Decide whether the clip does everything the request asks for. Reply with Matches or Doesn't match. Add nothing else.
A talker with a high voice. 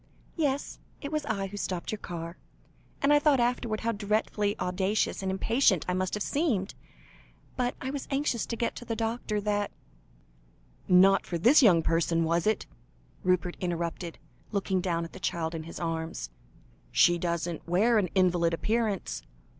Matches